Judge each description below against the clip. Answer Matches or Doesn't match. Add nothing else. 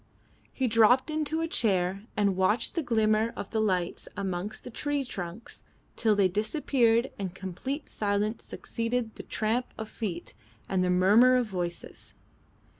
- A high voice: Matches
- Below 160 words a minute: Matches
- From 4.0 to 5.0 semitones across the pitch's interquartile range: Matches